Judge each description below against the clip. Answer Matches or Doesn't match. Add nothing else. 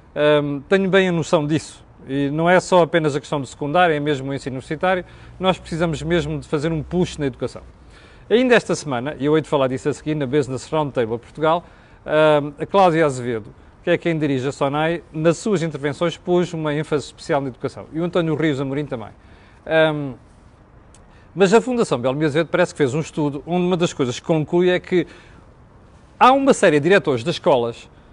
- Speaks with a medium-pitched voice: Matches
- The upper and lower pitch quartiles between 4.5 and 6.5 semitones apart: Doesn't match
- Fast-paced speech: Matches